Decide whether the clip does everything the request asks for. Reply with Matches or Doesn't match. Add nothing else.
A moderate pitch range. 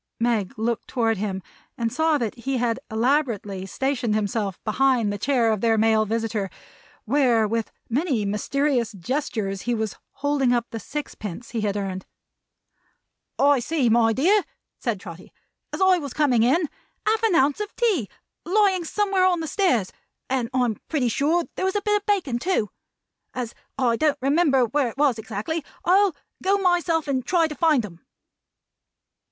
Doesn't match